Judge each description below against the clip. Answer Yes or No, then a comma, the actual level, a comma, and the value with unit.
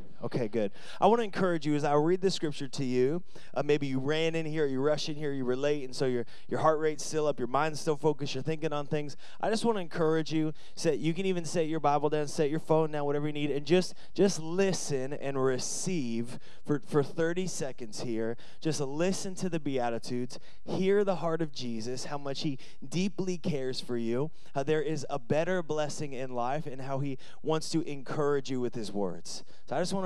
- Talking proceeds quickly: Yes, fast, 225 wpm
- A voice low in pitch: No, medium, 150 Hz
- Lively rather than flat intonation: No, average, 3.0 semitones